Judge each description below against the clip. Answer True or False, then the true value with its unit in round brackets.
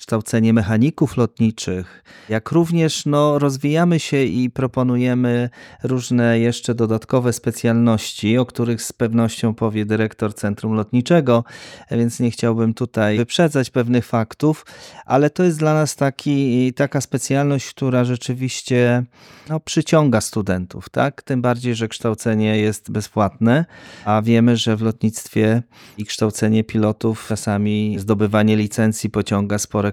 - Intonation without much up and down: False (3.0 semitones)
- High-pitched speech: False (120 Hz)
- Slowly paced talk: False (125 wpm)